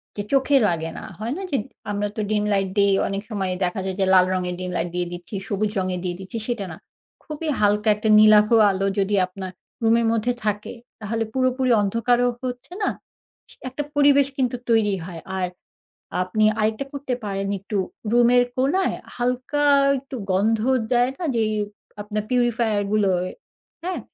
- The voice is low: No, high, 215 Hz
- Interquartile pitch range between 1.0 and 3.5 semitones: No, average, 4.0 semitones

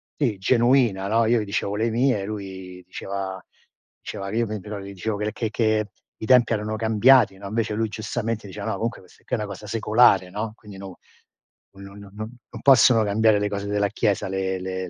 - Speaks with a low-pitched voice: Yes, low, 105 Hz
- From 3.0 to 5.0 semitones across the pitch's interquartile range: No, narrow, 2.4 semitones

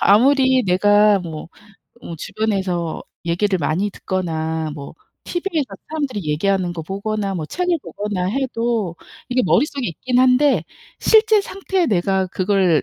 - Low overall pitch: No, high, 205 Hz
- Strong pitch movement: Yes, wide, 6.7 semitones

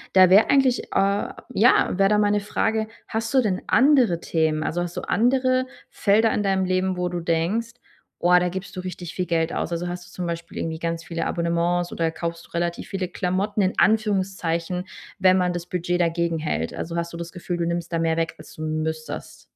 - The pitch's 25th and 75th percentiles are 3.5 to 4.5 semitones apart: No, average, 2.8 semitones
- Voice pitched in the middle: Yes, medium, 180 Hz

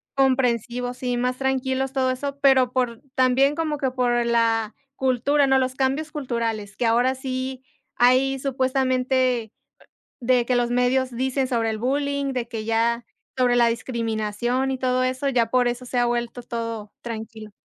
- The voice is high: Yes, very high, 250 Hz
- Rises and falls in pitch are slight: Yes, narrow, 1.9 semitones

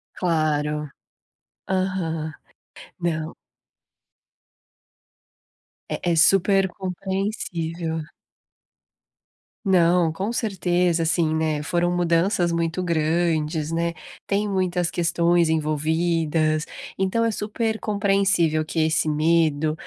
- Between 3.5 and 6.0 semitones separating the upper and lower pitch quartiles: No, average, 2.8 semitones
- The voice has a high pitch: No, medium, 170 Hz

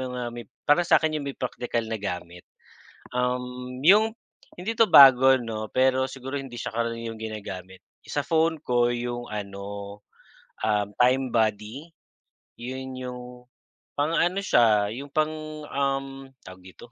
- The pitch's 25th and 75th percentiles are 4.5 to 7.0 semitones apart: No, average, 3.9 semitones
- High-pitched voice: No, low, 125 Hz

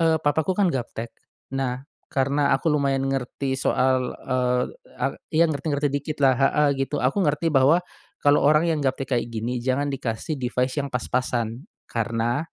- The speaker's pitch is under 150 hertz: Yes, low, 135 Hz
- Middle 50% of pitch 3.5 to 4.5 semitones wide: No, average, 2.8 semitones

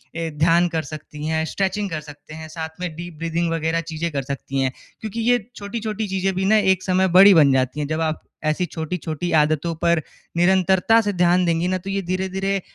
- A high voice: No, medium, 170 Hz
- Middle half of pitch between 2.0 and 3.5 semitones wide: Yes, average, 3.1 semitones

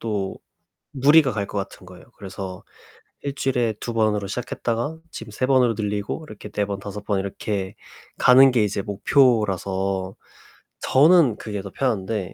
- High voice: No, low, 105 Hz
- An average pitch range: Yes, average, 4.1 semitones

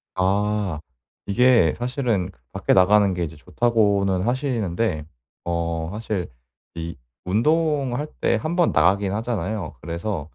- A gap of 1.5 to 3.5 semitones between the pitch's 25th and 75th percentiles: No, wide, 5.4 semitones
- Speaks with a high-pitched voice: No, low, 100 Hz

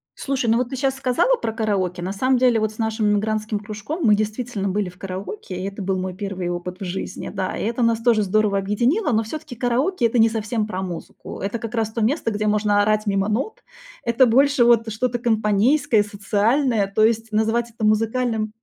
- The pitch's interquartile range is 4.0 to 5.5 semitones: No, average, 2.8 semitones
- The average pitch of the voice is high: Yes, high, 220 Hz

